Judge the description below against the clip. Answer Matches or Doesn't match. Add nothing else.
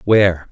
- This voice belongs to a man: Matches